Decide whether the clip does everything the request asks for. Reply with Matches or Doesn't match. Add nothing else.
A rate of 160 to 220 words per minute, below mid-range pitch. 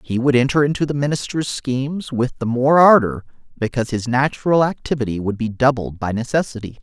Matches